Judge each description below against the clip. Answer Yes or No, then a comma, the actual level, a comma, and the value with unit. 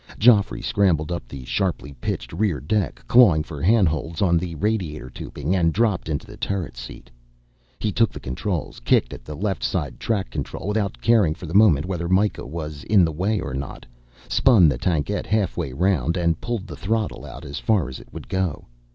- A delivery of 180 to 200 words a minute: Yes, average, 195 wpm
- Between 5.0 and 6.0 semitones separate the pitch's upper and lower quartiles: Yes, wide, 5.4 semitones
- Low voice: Yes, very low, 90 Hz